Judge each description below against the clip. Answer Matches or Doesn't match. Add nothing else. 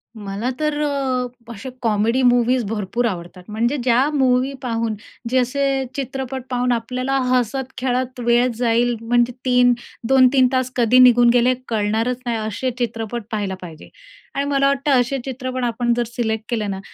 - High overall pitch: Matches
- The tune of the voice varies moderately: Doesn't match